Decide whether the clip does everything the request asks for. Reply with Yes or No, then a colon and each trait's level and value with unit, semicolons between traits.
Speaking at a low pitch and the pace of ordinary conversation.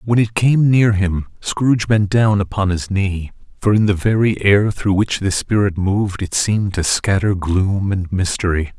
Yes: low, 100 Hz; average, 190 wpm